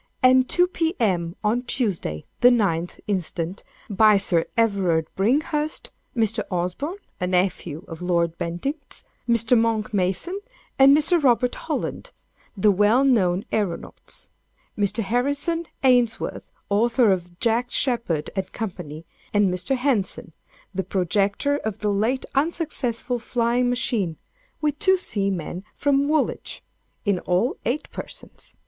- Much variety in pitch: Yes, wide, 5.9 semitones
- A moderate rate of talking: No, slow, 115 wpm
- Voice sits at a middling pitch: No, high, 220 Hz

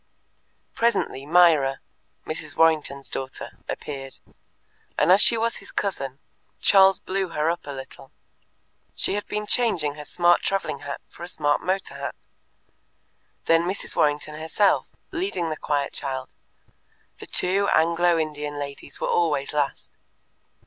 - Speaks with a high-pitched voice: No, medium, 160 Hz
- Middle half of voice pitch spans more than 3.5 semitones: Yes, average, 4.3 semitones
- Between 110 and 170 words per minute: Yes, slow, 135 wpm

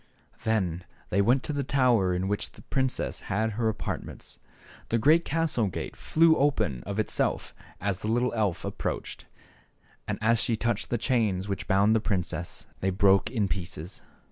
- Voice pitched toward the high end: No, low, 110 Hz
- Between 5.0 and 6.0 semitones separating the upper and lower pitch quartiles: No, average, 4.1 semitones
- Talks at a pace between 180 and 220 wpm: No, average, 170 wpm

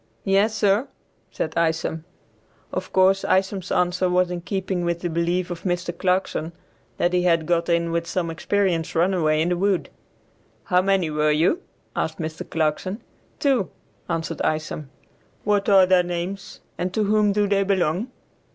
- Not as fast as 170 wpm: Yes, average, 160 wpm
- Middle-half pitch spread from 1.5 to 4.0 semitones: Yes, narrow, 2.6 semitones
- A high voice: No, medium, 180 Hz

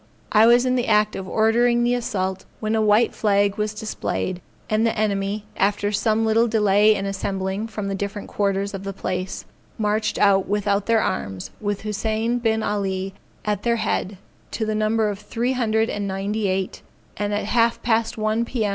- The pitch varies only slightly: Yes, narrow, 2.0 semitones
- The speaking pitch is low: No, high, 210 Hz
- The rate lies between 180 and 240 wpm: Yes, average, 185 wpm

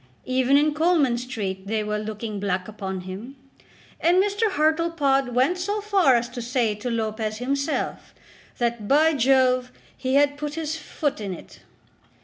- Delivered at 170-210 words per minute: No, average, 155 wpm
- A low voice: No, very high, 255 Hz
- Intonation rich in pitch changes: Yes, wide, 5.8 semitones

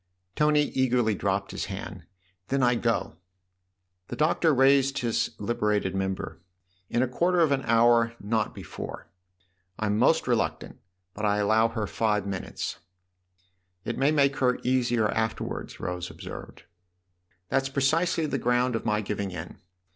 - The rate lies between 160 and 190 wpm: No, average, 150 wpm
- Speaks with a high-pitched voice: No, low, 115 Hz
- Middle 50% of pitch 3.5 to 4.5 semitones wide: No, average, 5.2 semitones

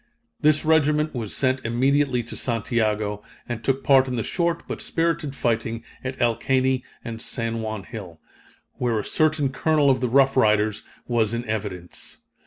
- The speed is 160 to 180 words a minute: Yes, average, 165 wpm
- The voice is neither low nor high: No, low, 125 Hz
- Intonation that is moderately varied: Yes, average, 3.7 semitones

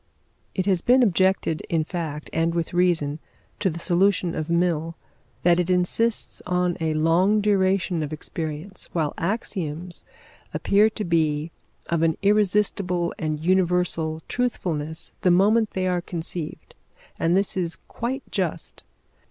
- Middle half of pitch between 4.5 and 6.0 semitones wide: No, average, 2.9 semitones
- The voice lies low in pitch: No, medium, 175 Hz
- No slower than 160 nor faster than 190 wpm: No, slow, 135 wpm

